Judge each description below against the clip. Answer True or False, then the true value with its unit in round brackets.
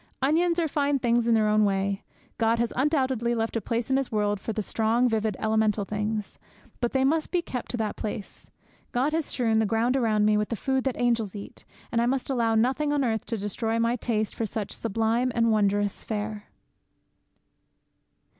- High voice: True (230 Hz)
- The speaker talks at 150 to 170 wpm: False (200 wpm)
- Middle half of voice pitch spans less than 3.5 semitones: True (2.9 semitones)